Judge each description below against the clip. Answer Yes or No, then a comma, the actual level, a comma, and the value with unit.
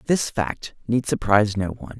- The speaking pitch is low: Yes, low, 110 Hz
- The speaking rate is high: No, average, 180 wpm